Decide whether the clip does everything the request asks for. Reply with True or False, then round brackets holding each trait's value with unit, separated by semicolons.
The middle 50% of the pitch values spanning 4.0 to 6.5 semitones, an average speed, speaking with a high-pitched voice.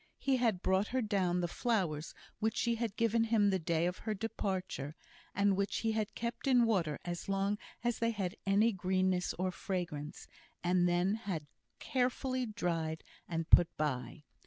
True (4.3 semitones; 170 wpm; 195 Hz)